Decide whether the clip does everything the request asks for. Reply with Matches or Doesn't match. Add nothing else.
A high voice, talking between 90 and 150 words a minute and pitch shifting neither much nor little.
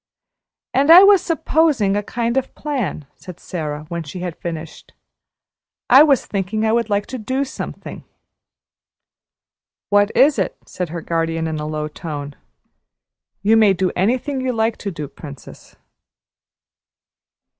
Doesn't match